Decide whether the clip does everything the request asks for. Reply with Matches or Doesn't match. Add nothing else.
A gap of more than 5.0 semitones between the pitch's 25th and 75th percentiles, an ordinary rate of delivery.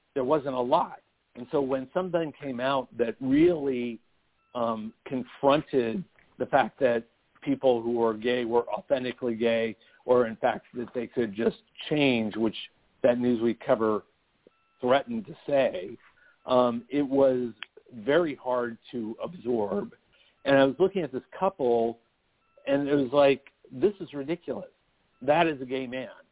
Doesn't match